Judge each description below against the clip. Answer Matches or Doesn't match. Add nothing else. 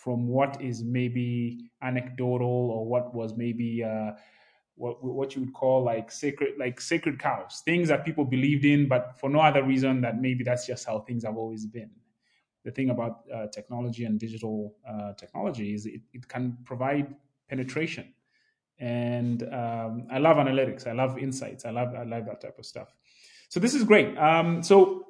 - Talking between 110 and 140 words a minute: Doesn't match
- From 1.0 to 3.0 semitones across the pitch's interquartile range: Matches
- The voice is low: Matches